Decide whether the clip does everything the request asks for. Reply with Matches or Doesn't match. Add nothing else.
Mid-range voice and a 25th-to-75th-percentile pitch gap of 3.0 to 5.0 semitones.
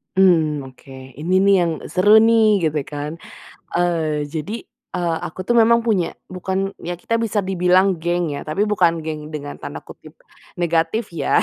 Matches